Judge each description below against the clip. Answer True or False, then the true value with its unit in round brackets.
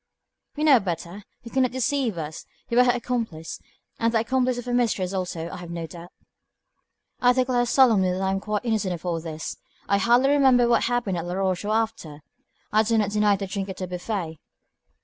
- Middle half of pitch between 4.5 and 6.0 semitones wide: True (5.1 semitones)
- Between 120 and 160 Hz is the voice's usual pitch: False (210 Hz)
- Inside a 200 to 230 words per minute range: True (205 wpm)